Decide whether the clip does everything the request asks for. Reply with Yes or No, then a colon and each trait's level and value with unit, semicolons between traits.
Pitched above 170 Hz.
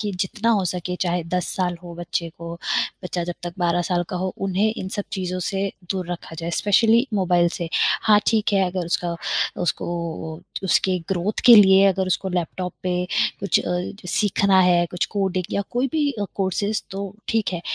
Yes: medium, 185 Hz